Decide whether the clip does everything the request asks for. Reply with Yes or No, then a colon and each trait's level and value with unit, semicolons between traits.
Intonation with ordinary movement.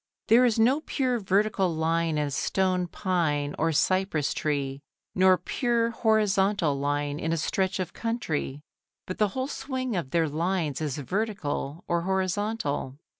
No: wide, 6.0 semitones